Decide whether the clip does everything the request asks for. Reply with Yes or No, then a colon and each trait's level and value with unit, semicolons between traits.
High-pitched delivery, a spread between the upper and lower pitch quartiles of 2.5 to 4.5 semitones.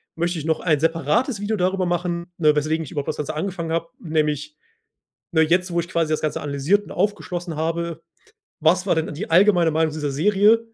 No: medium, 165 Hz; average, 2.9 semitones